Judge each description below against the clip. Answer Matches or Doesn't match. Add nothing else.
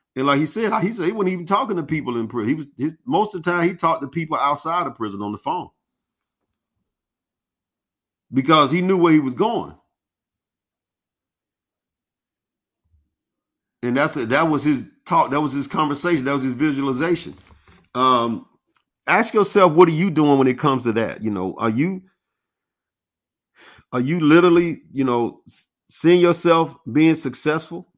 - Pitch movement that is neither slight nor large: Doesn't match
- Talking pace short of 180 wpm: Matches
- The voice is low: Doesn't match